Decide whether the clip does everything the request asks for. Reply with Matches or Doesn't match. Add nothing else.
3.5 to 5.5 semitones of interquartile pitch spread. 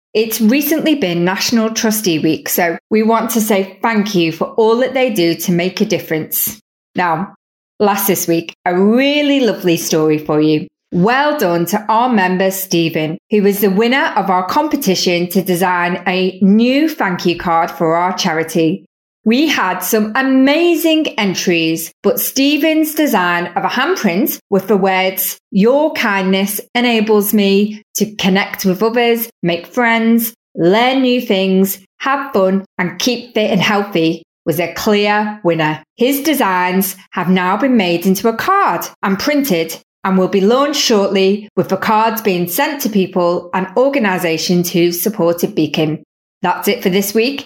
Matches